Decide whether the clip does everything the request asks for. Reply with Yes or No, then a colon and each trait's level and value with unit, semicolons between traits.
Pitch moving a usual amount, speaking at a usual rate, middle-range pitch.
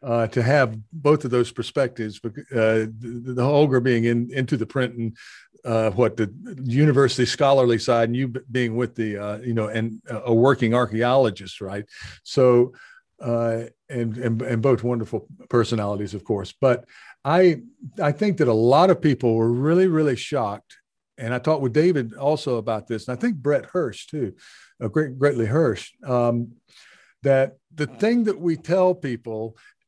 No: average, 4.0 semitones; average, 170 wpm; low, 125 Hz